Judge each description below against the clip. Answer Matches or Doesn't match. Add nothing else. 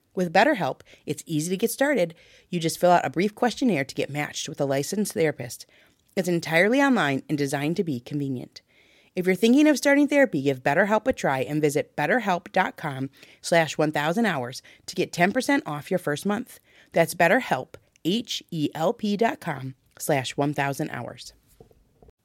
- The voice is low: Doesn't match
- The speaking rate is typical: Matches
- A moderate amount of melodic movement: Doesn't match